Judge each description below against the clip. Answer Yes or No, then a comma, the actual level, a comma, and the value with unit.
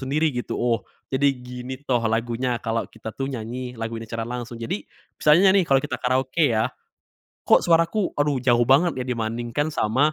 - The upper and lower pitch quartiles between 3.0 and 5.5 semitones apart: Yes, average, 3.4 semitones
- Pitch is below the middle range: Yes, low, 125 Hz